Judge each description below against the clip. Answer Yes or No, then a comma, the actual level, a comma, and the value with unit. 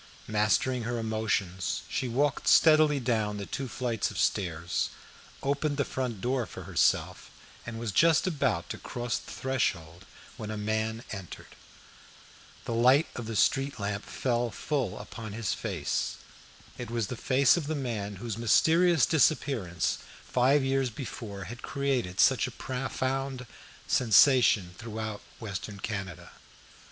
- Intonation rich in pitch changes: No, average, 4.2 semitones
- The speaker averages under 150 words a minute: Yes, average, 140 wpm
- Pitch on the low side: Yes, low, 120 Hz